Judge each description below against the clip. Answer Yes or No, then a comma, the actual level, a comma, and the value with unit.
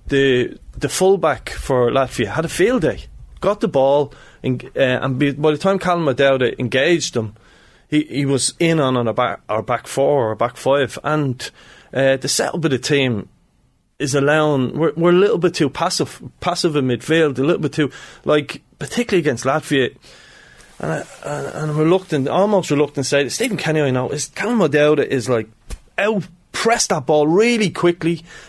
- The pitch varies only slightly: No, average, 4.1 semitones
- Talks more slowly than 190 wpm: Yes, average, 180 wpm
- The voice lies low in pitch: No, medium, 145 Hz